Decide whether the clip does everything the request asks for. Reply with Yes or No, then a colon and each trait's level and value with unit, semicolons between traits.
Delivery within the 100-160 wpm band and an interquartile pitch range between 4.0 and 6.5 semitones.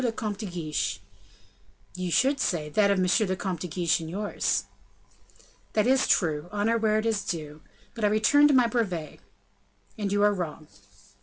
No: average, 180 wpm; average, 4.4 semitones